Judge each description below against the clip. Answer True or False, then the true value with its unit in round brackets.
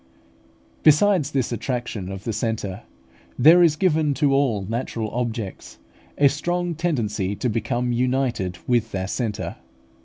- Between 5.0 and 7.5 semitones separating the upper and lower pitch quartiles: True (5.3 semitones)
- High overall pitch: False (120 Hz)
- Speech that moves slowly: True (130 wpm)